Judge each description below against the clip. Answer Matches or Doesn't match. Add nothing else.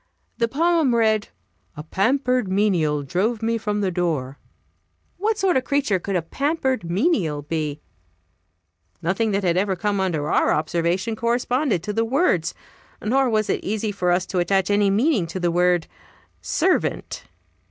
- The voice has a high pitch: Matches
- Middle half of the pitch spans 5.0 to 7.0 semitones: Matches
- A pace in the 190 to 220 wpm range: Doesn't match